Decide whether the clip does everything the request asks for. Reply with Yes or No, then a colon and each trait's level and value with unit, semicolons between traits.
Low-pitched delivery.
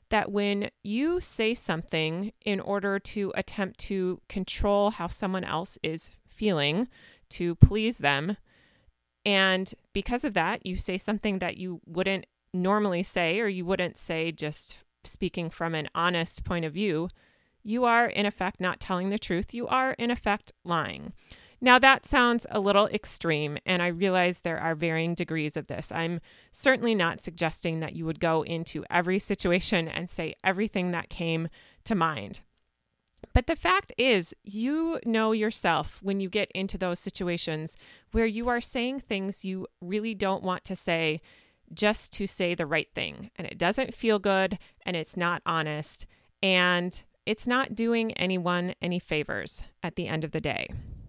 No: medium, 185 Hz